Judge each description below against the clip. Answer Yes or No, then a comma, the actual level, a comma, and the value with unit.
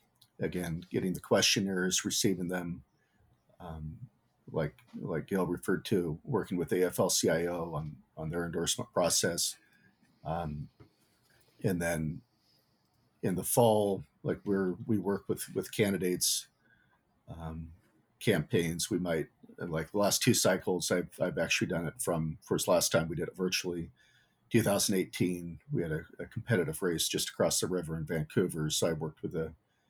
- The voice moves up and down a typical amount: No, narrow, 2.3 semitones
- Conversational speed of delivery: Yes, average, 145 wpm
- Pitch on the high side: No, very low, 85 Hz